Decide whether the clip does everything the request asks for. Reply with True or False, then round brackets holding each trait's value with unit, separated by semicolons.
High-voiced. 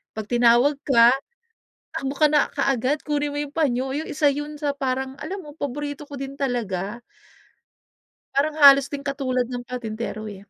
True (275 Hz)